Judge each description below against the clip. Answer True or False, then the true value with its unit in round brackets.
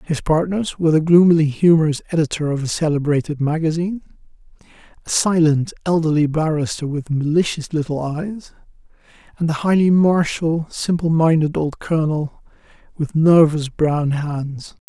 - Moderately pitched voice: True (160 Hz)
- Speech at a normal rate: False (125 wpm)